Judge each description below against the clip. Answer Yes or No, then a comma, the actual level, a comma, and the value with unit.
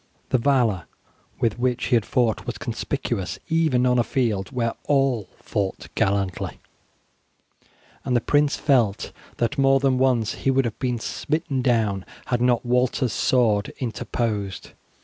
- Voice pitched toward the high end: No, low, 120 Hz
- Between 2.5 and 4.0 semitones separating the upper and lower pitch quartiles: Yes, average, 3.2 semitones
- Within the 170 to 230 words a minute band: No, average, 145 wpm